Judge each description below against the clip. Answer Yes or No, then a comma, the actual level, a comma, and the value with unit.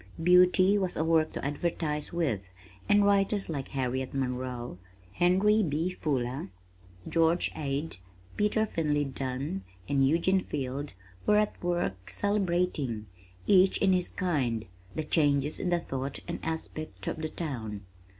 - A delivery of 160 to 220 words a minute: No, slow, 135 wpm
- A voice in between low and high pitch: Yes, medium, 155 Hz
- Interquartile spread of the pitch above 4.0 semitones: Yes, average, 5.2 semitones